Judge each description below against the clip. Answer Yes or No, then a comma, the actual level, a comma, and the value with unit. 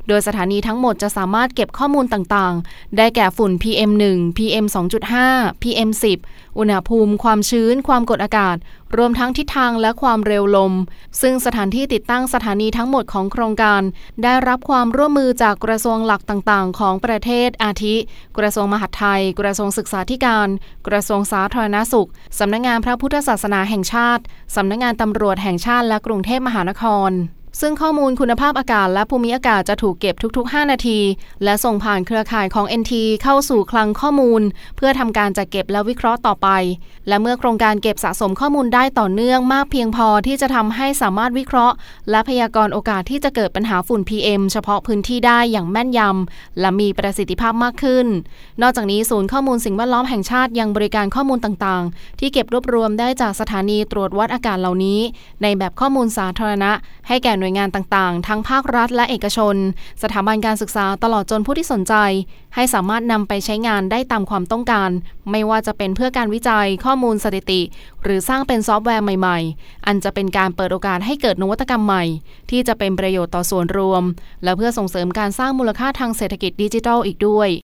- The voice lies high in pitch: Yes, high, 215 Hz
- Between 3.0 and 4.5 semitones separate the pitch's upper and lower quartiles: Yes, average, 3.3 semitones